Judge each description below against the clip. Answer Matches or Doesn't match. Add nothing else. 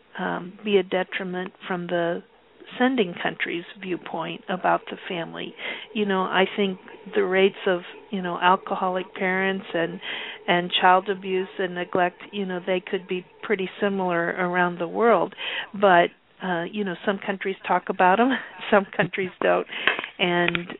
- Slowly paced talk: Doesn't match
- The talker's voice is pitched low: Doesn't match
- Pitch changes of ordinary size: Doesn't match